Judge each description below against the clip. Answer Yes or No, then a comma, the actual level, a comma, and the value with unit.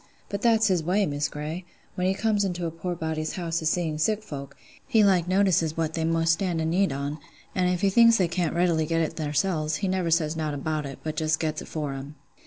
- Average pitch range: Yes, average, 3.1 semitones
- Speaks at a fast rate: Yes, fast, 240 wpm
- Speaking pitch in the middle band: Yes, medium, 165 Hz